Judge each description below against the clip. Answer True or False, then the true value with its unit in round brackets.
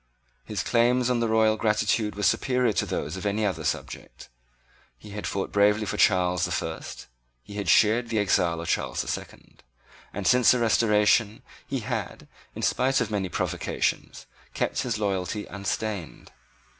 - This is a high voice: False (105 Hz)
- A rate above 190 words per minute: False (165 wpm)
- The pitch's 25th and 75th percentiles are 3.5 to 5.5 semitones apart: False (3.0 semitones)